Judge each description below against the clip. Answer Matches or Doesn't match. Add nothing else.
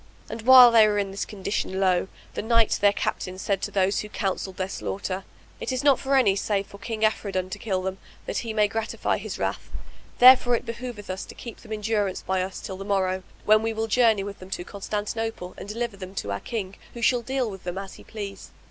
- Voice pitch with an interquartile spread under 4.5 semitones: Matches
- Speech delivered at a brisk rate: Matches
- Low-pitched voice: Doesn't match